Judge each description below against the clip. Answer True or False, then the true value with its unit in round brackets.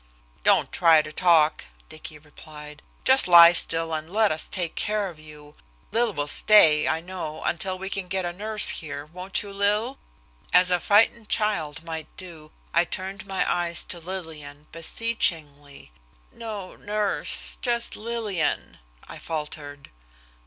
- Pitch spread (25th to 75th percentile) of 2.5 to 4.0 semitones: False (4.7 semitones)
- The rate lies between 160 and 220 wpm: False (145 wpm)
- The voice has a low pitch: False (175 Hz)